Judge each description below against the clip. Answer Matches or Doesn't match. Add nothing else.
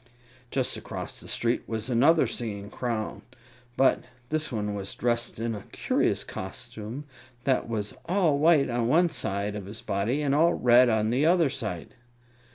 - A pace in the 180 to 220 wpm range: Doesn't match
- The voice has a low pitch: Matches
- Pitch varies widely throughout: Doesn't match